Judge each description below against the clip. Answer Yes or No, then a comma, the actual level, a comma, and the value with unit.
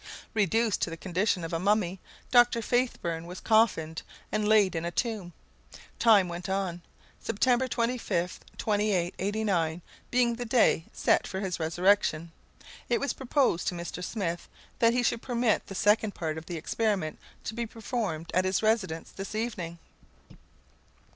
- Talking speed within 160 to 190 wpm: No, average, 150 wpm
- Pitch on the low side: No, high, 200 Hz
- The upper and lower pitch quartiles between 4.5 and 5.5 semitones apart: Yes, average, 4.8 semitones